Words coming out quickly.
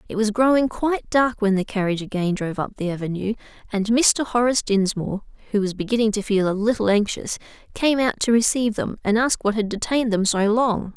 Yes: fast, 210 wpm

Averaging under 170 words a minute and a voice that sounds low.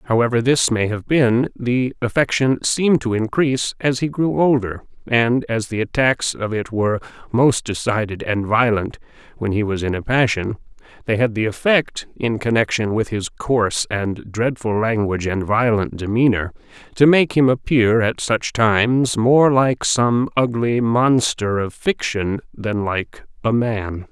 Yes: average, 160 wpm; low, 115 Hz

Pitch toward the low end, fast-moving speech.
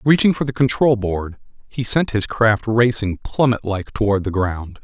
No: low, 115 Hz; average, 185 wpm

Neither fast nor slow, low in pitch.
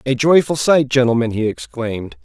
Yes: average, 160 wpm; low, 130 Hz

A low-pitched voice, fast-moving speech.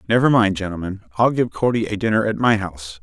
Yes: low, 105 Hz; fast, 220 wpm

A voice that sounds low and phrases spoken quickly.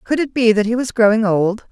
No: high, 225 Hz; fast, 280 wpm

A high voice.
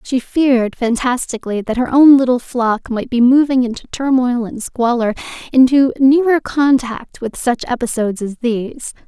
Yes: very high, 250 Hz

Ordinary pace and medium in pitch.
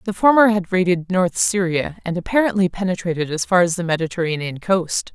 Yes: average, 175 wpm; medium, 180 Hz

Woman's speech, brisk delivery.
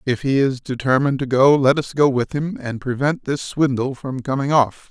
No: male; fast, 220 wpm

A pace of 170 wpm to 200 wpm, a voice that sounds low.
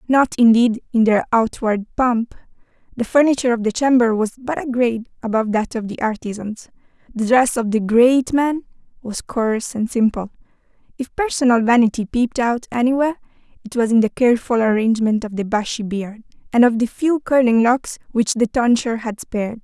No: average, 175 wpm; high, 235 Hz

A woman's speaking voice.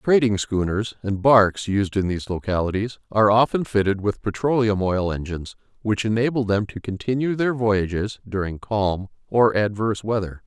No: male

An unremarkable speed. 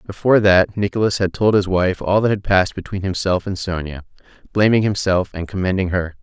Yes: average, 195 wpm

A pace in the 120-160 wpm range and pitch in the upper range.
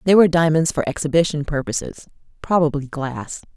No: slow, 135 wpm; medium, 155 Hz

